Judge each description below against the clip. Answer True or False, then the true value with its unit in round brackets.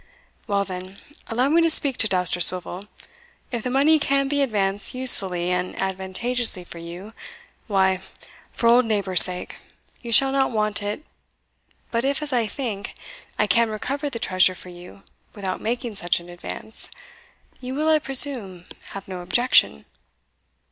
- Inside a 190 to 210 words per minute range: False (155 wpm)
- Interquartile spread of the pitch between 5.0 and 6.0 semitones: True (5.5 semitones)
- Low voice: False (210 Hz)